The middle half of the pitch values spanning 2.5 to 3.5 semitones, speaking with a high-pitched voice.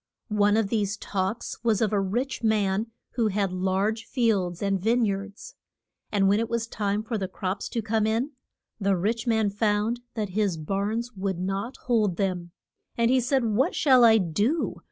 Yes: average, 2.8 semitones; high, 210 Hz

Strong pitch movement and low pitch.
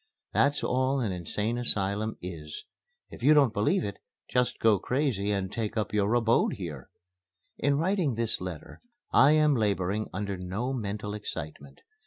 No: average, 4.5 semitones; low, 105 Hz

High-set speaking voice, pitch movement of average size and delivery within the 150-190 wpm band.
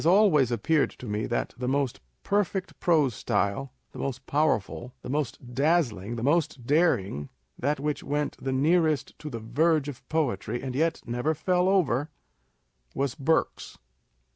No: medium, 140 Hz; average, 4.6 semitones; average, 160 wpm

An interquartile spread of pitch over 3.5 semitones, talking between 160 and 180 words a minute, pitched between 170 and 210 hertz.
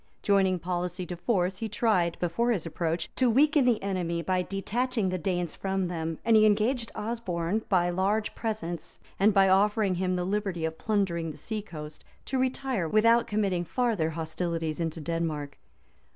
Yes: average, 4.2 semitones; average, 165 wpm; medium, 185 Hz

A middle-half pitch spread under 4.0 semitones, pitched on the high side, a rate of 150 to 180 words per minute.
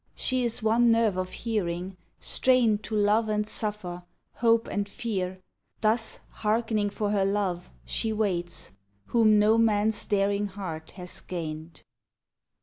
No: average, 3.1 semitones; high, 210 Hz; slow, 135 wpm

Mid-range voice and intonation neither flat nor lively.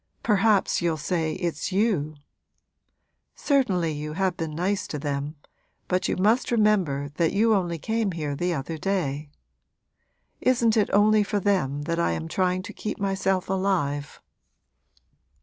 Yes: medium, 180 Hz; average, 4.8 semitones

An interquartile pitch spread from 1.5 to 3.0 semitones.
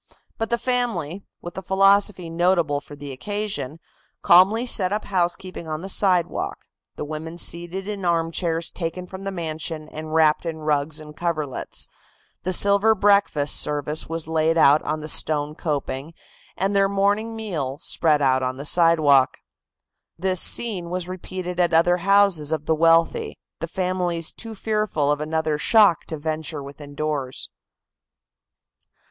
No: average, 3.9 semitones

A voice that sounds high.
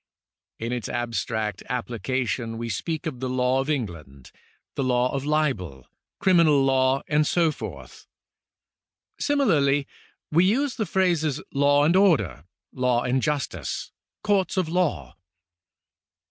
No: low, 135 Hz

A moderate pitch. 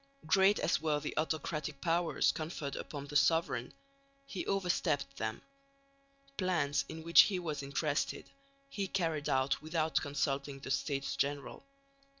Yes: medium, 155 Hz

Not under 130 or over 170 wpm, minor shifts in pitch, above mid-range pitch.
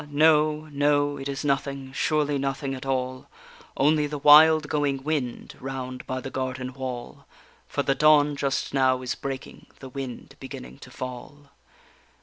No: average, 150 wpm; narrow, 2.1 semitones; low, 135 Hz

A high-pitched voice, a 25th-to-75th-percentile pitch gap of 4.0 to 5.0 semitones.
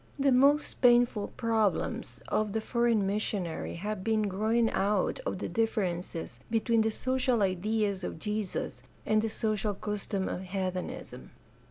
No: high, 215 Hz; average, 2.8 semitones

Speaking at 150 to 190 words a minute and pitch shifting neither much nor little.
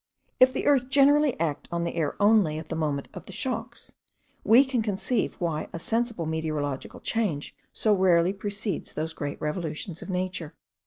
No: average, 170 wpm; wide, 5.9 semitones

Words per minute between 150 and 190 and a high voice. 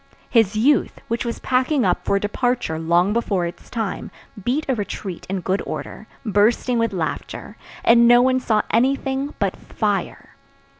Yes: average, 155 wpm; high, 230 Hz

